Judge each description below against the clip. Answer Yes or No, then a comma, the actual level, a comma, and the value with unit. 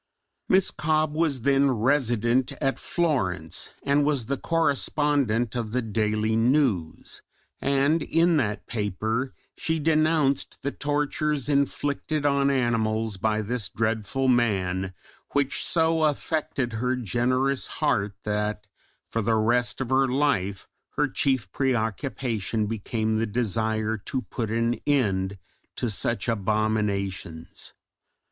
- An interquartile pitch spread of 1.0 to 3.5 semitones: No, average, 4.5 semitones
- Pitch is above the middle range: No, low, 120 Hz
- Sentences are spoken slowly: Yes, slow, 120 wpm